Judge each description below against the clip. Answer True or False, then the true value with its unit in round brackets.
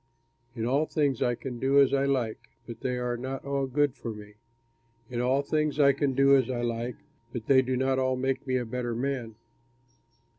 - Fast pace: True (210 wpm)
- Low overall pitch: True (130 Hz)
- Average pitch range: False (2.2 semitones)